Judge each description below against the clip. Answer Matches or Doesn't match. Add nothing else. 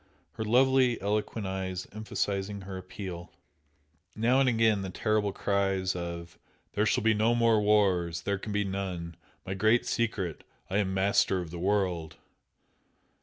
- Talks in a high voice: Doesn't match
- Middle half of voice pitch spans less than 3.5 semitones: Matches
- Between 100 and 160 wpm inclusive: Matches